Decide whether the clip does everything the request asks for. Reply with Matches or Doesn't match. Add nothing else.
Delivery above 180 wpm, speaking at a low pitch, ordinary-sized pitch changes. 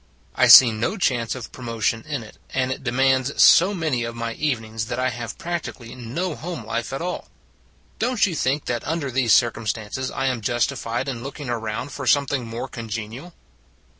Matches